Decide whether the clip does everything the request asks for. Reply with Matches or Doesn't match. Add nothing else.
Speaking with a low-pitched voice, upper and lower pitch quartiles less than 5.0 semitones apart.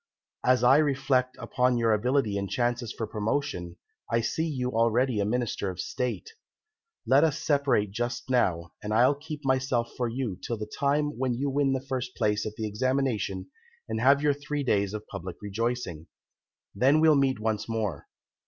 Matches